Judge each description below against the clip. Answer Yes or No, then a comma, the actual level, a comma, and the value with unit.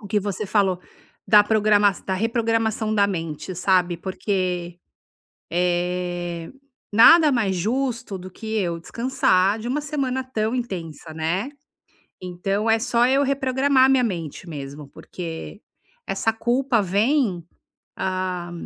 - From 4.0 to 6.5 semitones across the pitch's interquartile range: Yes, average, 4.8 semitones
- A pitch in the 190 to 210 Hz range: Yes, high, 200 Hz